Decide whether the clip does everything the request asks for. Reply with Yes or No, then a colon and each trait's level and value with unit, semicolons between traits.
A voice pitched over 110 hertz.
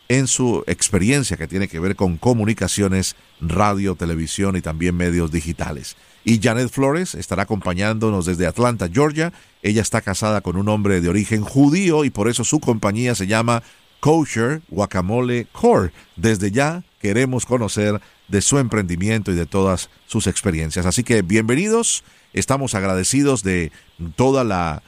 No: low, 105 Hz